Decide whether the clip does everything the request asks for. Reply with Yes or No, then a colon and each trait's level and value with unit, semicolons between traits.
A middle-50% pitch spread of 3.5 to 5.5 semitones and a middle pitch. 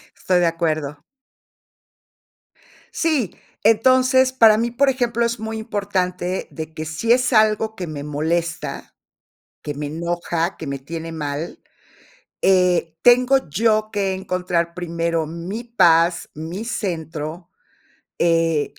Yes: average, 5.2 semitones; medium, 180 Hz